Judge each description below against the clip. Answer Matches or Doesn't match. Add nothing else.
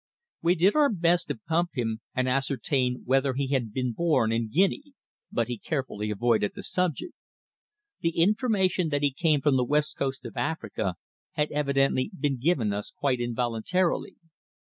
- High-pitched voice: Doesn't match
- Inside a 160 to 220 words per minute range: Matches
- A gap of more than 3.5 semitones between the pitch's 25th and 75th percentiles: Matches